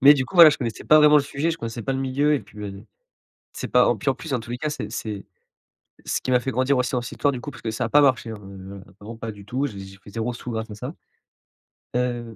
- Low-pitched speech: Yes, low, 125 Hz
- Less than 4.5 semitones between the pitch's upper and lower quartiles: Yes, average, 4.0 semitones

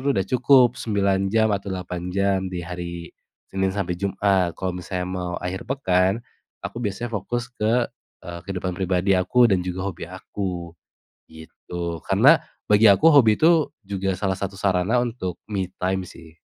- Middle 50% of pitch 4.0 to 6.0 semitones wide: No, narrow, 2.4 semitones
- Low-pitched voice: Yes, very low, 95 Hz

